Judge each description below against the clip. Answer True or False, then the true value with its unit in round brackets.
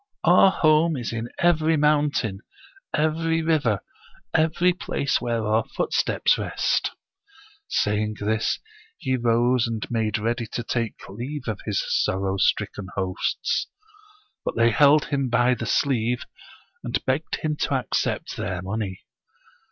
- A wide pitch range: True (5.7 semitones)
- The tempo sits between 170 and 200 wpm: False (135 wpm)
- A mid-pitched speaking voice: False (120 Hz)